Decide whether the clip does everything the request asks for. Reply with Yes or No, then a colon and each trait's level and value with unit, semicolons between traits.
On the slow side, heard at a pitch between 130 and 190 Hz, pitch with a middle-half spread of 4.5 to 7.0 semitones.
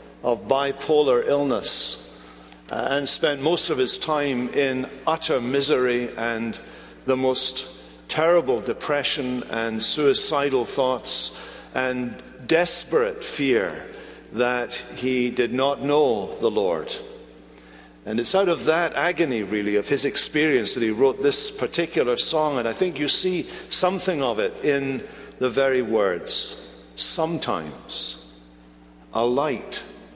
Yes: slow, 120 wpm; medium, 140 Hz; average, 5.0 semitones